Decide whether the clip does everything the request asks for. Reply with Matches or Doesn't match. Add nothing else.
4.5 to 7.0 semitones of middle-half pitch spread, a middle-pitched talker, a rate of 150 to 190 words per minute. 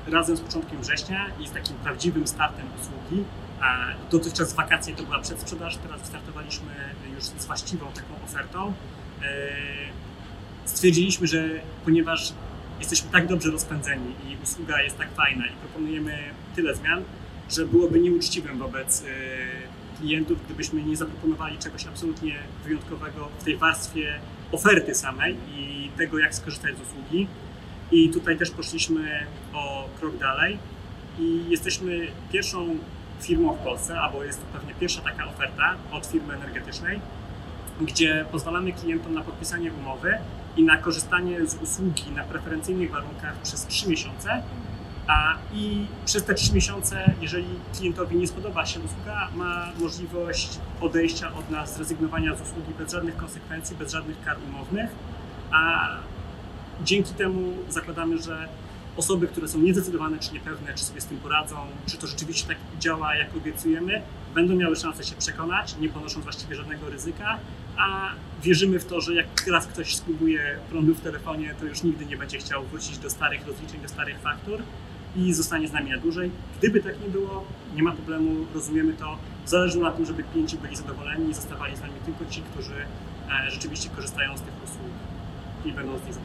Doesn't match